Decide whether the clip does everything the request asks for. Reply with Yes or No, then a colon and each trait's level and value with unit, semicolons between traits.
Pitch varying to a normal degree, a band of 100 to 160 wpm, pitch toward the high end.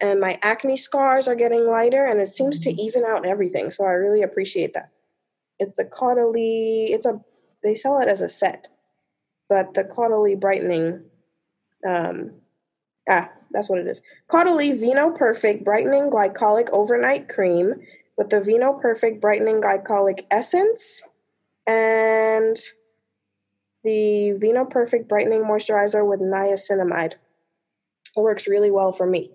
Yes: average, 3.6 semitones; average, 140 wpm; high, 215 Hz